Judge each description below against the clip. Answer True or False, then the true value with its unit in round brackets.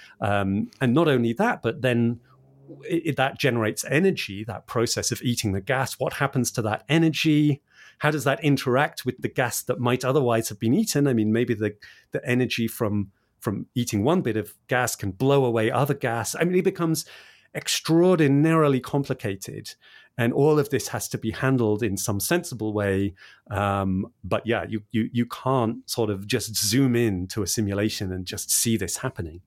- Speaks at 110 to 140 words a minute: False (185 wpm)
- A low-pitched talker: True (120 Hz)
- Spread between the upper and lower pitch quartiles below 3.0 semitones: False (4.0 semitones)